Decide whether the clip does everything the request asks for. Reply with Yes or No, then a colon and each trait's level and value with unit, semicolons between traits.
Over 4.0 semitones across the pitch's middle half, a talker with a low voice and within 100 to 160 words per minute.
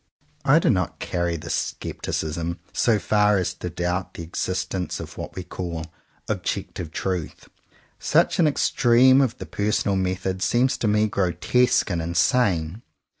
No: average, 3.7 semitones; very low, 95 Hz; average, 150 wpm